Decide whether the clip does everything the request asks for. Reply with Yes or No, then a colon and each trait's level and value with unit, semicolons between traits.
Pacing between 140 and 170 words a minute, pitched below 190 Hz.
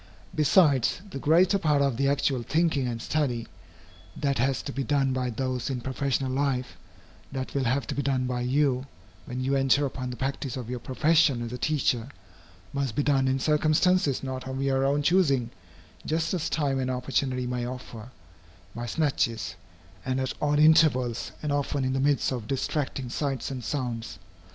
No: average, 180 wpm; low, 135 Hz